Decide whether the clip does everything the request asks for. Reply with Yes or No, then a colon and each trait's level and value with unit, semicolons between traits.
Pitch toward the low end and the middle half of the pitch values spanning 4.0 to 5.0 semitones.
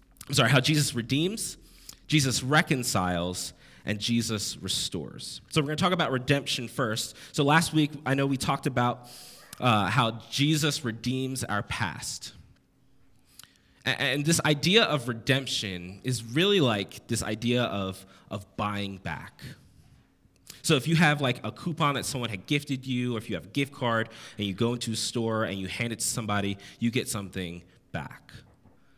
Yes: low, 125 Hz; average, 4.7 semitones